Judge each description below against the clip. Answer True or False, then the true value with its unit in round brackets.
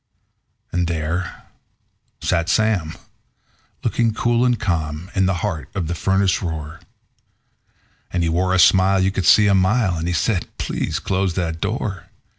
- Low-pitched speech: True (95 Hz)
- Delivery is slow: False (155 wpm)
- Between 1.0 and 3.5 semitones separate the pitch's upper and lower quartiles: True (2.9 semitones)